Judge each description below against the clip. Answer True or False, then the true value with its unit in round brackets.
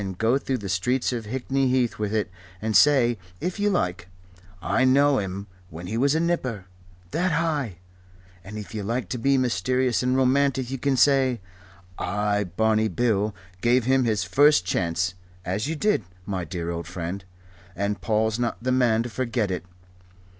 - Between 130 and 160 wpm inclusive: False (175 wpm)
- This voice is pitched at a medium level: False (115 Hz)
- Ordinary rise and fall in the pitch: True (4.7 semitones)